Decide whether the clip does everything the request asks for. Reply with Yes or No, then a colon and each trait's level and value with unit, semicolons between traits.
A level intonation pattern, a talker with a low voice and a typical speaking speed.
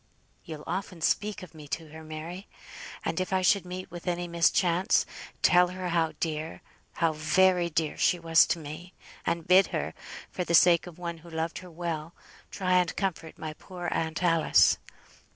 No: narrow, 2.1 semitones; medium, 170 Hz; average, 180 wpm